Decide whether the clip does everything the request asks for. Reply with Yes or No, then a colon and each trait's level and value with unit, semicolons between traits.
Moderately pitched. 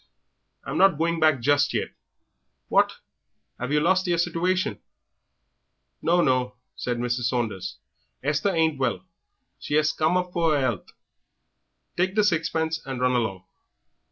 Yes: medium, 155 Hz